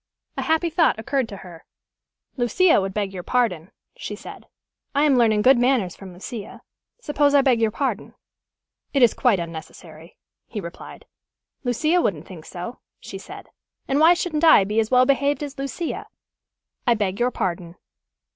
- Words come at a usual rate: Yes, average, 165 wpm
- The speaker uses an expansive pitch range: Yes, wide, 6.7 semitones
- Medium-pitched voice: No, high, 240 Hz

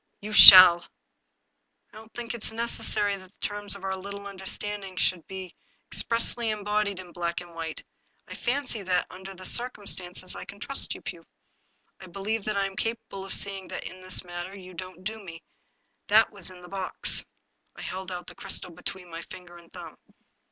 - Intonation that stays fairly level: Yes, narrow, 2.3 semitones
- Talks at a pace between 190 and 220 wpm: Yes, average, 195 wpm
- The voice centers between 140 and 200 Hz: Yes, high, 190 Hz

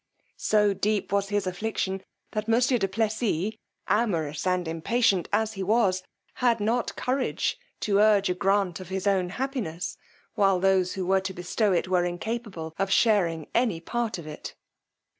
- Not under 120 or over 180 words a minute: Yes, average, 160 wpm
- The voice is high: Yes, high, 195 Hz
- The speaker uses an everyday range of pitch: Yes, average, 3.2 semitones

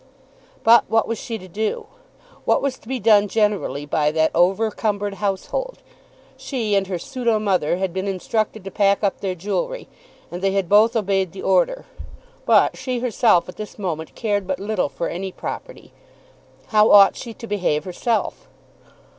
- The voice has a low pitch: No, high, 205 Hz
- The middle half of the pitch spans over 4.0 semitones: No, average, 3.2 semitones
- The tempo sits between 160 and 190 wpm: Yes, average, 170 wpm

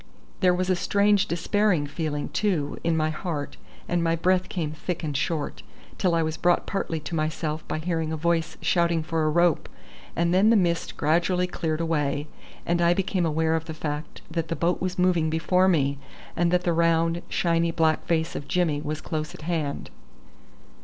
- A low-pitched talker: No, medium, 165 Hz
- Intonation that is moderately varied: No, narrow, 2.1 semitones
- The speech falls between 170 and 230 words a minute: Yes, average, 190 wpm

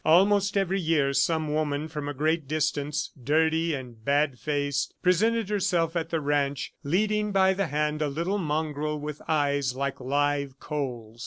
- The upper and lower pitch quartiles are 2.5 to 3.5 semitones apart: Yes, average, 2.9 semitones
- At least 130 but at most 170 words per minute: Yes, average, 160 wpm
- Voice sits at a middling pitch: Yes, medium, 150 Hz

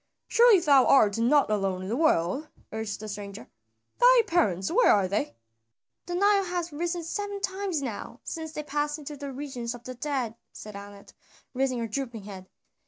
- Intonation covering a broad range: Yes, wide, 7.9 semitones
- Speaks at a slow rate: No, average, 175 wpm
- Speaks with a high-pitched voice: Yes, very high, 270 Hz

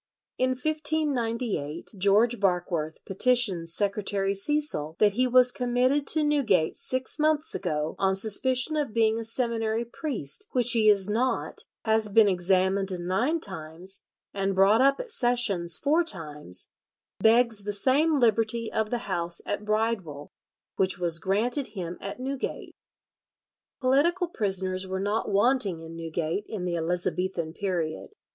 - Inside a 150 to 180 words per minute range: No, average, 140 wpm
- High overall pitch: Yes, high, 210 Hz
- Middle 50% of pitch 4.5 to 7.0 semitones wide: Yes, average, 5.2 semitones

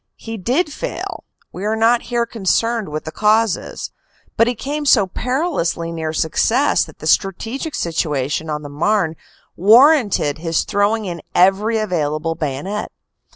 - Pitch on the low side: No, high, 205 Hz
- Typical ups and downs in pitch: No, wide, 6.1 semitones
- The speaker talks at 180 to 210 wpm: No, average, 145 wpm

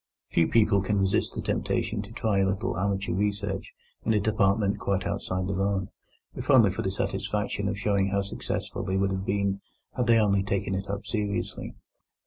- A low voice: Yes, low, 100 Hz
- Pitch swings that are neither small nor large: No, narrow, 1.1 semitones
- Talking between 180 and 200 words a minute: Yes, average, 190 wpm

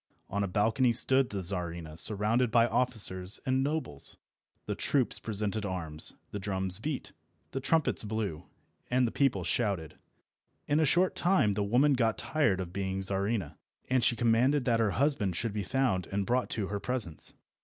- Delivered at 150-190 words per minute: Yes, average, 170 wpm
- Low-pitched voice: Yes, low, 110 Hz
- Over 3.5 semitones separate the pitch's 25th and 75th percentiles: Yes, average, 4.9 semitones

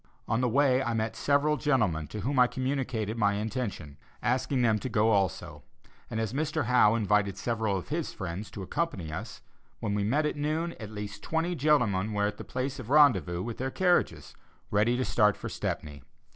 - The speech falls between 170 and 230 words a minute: Yes, average, 195 wpm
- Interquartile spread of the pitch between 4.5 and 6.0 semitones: Yes, average, 4.9 semitones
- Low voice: Yes, low, 115 Hz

